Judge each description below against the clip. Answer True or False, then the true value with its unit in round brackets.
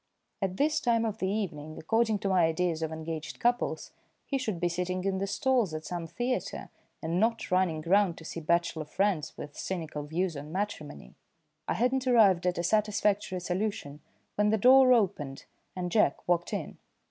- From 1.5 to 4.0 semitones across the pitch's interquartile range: False (4.8 semitones)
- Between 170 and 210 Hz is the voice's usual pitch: True (185 Hz)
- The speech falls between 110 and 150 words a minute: False (180 wpm)